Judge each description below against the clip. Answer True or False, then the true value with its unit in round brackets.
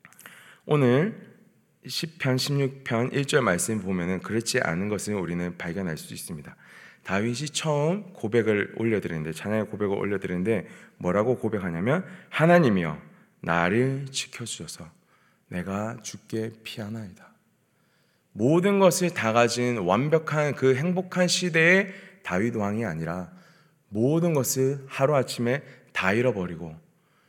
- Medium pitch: False (125 Hz)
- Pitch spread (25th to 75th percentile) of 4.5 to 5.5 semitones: False (6.3 semitones)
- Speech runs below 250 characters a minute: False (270 characters per minute)